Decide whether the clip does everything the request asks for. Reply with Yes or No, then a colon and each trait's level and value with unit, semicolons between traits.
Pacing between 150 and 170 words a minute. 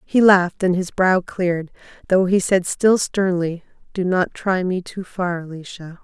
No: average, 180 wpm